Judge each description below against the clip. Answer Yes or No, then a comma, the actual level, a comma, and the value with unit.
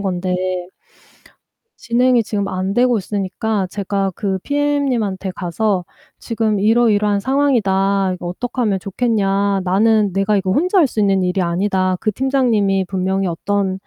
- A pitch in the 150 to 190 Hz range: No, high, 200 Hz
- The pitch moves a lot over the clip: No, average, 3.1 semitones